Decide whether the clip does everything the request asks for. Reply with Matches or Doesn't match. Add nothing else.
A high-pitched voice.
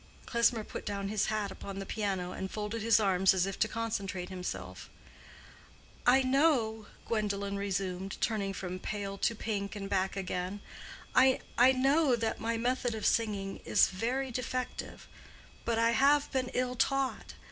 Matches